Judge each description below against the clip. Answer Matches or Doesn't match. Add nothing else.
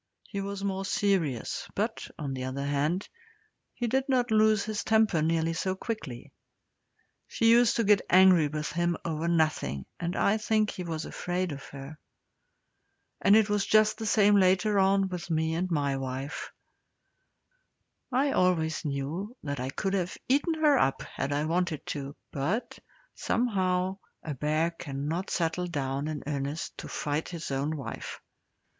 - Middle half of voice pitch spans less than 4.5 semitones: Doesn't match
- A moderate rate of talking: Matches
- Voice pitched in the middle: Matches